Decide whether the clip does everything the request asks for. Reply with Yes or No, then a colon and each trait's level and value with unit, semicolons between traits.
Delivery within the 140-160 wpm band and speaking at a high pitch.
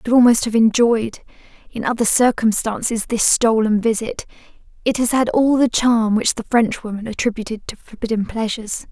Yes: average, 155 wpm; high, 225 Hz